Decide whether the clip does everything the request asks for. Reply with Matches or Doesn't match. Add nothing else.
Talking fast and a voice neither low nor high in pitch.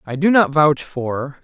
Matches